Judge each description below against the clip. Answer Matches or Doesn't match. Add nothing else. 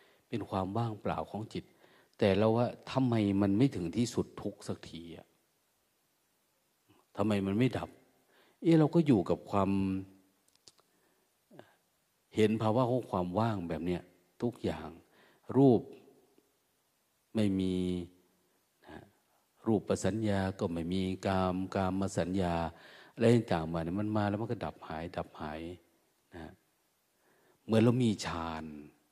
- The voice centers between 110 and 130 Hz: Doesn't match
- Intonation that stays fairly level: Doesn't match